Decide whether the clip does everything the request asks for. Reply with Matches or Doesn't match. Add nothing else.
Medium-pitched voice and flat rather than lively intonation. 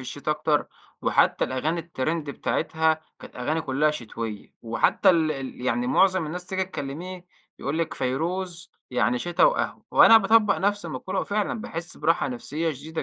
Doesn't match